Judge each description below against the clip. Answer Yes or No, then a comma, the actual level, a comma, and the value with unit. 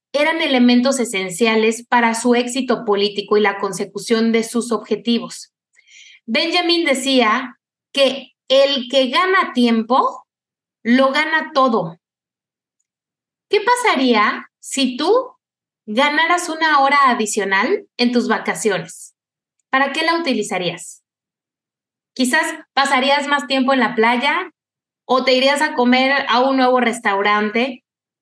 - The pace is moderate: No, slow, 115 wpm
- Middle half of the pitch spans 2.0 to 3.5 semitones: No, average, 4.0 semitones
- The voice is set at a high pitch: Yes, very high, 255 Hz